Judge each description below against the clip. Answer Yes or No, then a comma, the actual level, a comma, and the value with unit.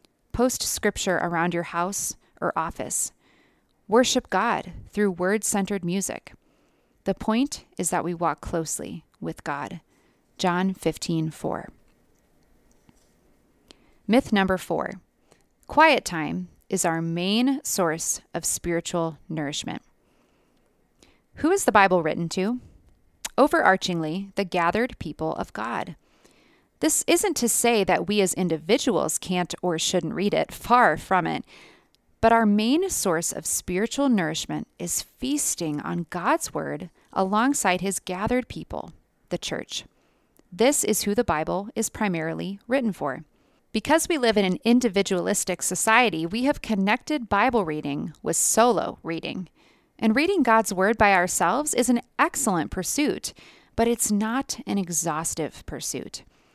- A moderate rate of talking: No, slow, 130 wpm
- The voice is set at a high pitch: Yes, high, 200 Hz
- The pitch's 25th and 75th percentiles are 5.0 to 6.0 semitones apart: Yes, average, 5.3 semitones